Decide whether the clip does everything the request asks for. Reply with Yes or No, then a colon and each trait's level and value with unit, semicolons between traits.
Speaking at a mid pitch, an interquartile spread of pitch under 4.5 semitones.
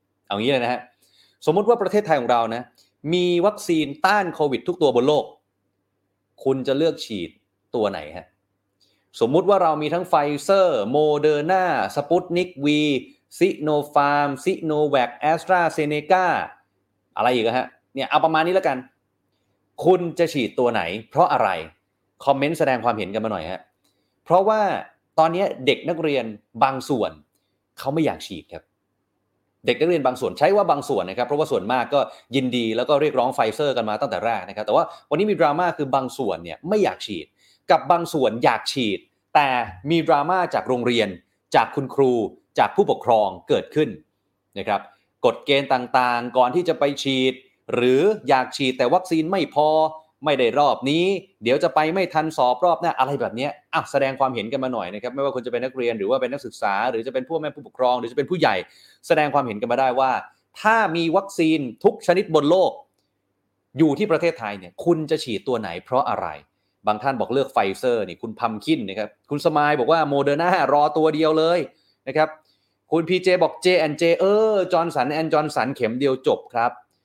No: medium, 145 Hz; wide, 5.6 semitones